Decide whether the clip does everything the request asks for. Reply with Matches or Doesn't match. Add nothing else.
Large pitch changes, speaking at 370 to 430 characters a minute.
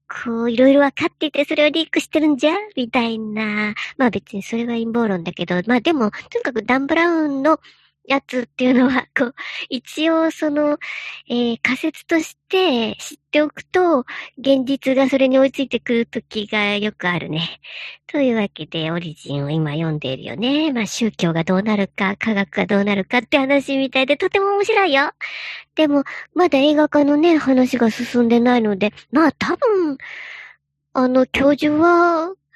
Doesn't match